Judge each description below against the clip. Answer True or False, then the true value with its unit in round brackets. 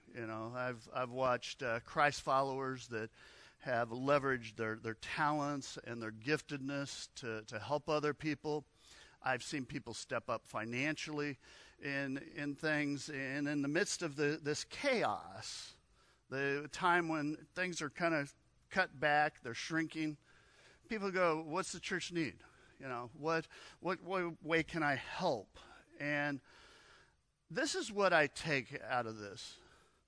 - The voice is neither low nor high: True (145 Hz)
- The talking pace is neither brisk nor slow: True (150 wpm)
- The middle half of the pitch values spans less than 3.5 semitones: False (3.9 semitones)